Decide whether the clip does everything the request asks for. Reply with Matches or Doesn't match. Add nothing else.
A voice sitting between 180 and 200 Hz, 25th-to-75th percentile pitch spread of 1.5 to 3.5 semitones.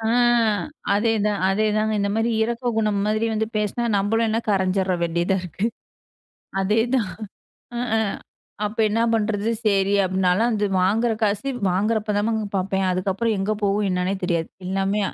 Doesn't match